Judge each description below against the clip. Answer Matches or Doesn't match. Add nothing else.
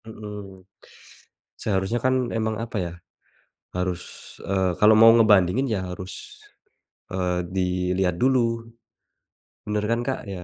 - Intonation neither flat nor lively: Matches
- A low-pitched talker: Matches